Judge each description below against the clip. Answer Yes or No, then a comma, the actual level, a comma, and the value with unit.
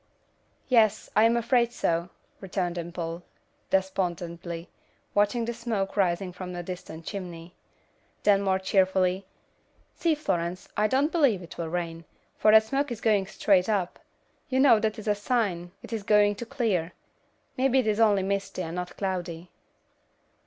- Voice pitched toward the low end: No, high, 195 Hz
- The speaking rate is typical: Yes, average, 155 wpm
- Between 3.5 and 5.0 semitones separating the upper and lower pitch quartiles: Yes, average, 3.9 semitones